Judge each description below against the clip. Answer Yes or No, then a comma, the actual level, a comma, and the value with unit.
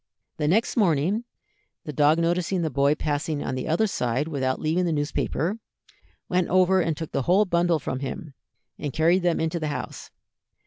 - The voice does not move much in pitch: No, average, 3.5 semitones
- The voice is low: No, medium, 160 Hz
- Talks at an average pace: Yes, average, 180 wpm